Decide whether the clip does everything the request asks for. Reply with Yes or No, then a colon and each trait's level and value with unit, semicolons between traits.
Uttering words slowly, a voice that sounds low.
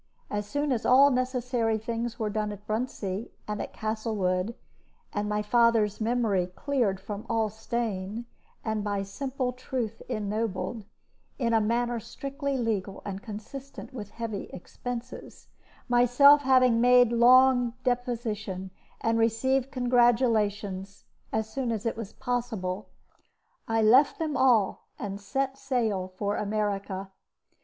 No: slow, 130 wpm; high, 225 Hz